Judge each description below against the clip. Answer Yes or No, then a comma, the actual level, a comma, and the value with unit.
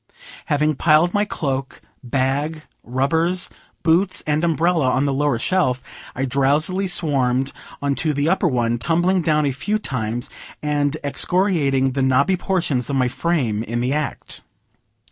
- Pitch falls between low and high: Yes, medium, 145 Hz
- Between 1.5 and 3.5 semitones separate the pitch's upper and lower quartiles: No, average, 4.2 semitones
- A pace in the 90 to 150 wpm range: Yes, average, 145 wpm